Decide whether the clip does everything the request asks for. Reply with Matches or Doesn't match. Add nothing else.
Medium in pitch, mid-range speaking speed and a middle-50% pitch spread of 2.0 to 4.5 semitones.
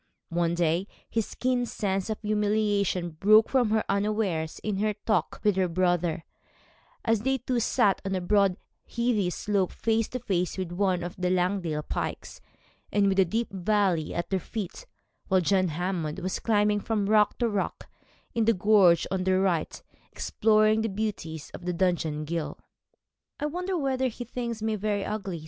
Doesn't match